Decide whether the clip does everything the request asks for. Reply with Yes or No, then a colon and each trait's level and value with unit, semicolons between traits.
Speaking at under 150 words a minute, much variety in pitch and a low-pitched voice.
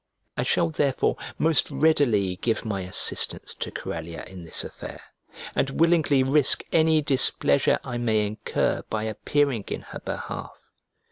Yes: average, 140 wpm; wide, 6.5 semitones; low, 120 Hz